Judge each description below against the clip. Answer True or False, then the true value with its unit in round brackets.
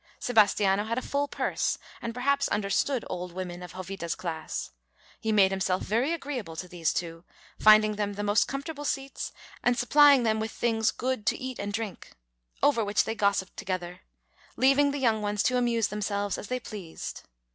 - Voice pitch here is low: False (215 Hz)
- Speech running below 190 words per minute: True (180 wpm)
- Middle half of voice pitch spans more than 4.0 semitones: True (4.6 semitones)